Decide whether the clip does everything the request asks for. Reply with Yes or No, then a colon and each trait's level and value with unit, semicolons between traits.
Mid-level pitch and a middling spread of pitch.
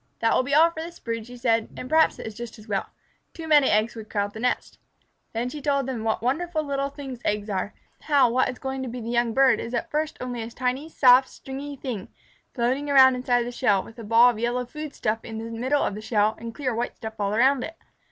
No: high, 245 Hz; average, 3.4 semitones